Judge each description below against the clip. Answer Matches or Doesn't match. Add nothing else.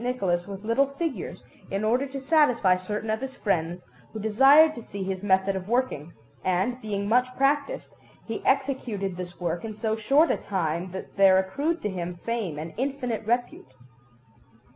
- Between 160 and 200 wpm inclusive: Matches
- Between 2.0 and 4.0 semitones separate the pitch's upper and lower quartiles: Doesn't match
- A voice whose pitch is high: Matches